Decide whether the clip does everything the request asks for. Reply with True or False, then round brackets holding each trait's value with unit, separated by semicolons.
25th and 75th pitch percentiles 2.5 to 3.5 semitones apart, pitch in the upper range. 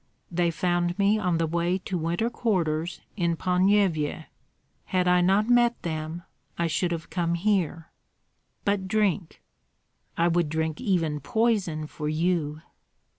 False (3.0 semitones; 175 Hz)